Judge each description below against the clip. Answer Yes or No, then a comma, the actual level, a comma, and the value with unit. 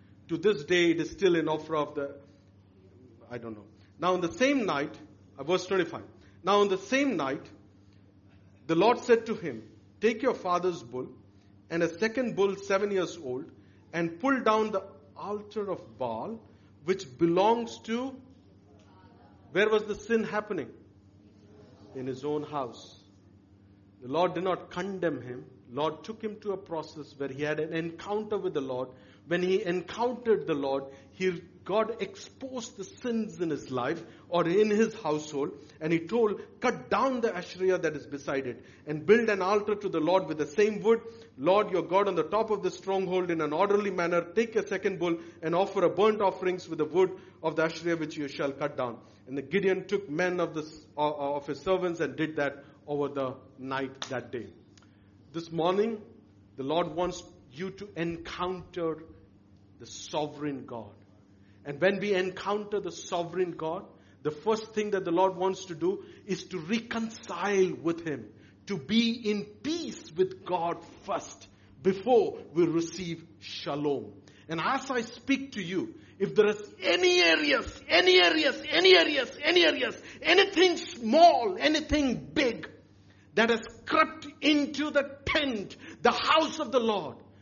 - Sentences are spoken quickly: No, average, 170 wpm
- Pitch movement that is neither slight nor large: No, wide, 7.4 semitones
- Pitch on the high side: No, medium, 175 Hz